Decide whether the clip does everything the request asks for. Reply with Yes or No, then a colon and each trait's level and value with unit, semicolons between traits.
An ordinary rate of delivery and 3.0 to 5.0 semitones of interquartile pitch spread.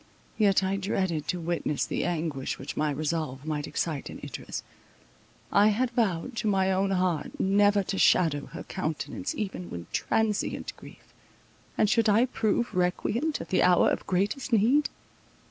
Yes: average, 160 wpm; average, 4.5 semitones